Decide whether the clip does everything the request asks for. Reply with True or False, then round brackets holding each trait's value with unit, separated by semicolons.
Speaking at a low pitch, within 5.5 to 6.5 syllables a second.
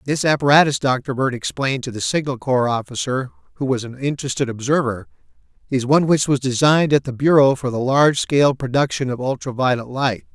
True (130 Hz; 5.9 syllables/s)